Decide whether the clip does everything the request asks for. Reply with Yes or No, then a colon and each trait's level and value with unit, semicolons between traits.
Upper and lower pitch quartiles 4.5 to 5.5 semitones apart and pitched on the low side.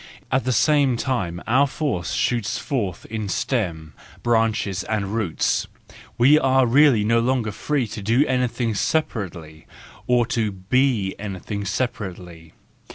Yes: average, 4.9 semitones; low, 115 Hz